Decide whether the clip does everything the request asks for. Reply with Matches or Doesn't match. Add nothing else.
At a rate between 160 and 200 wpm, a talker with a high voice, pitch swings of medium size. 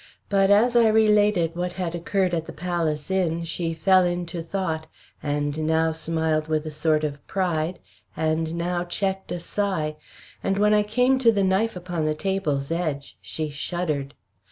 Doesn't match